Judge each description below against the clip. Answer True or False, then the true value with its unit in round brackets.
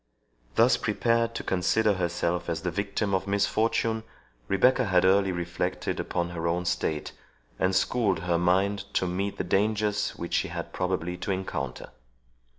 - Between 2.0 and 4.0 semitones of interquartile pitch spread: True (2.6 semitones)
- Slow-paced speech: False (155 wpm)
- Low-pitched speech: True (95 Hz)